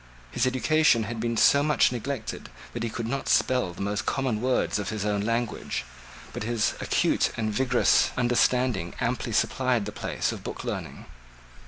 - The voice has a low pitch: Yes, low, 115 Hz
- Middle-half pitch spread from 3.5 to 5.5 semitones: No, average, 3.0 semitones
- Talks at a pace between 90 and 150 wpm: No, average, 170 wpm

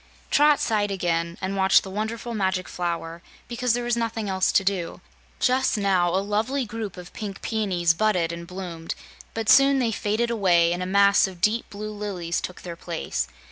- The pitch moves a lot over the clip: No, average, 3.9 semitones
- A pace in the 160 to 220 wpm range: Yes, average, 185 wpm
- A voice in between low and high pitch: No, high, 200 Hz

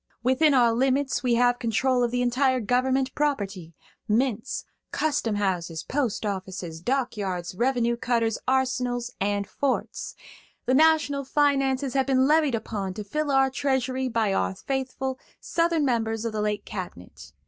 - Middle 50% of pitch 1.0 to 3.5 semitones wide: No, average, 4.1 semitones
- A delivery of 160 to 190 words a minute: No, average, 145 wpm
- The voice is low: No, high, 245 Hz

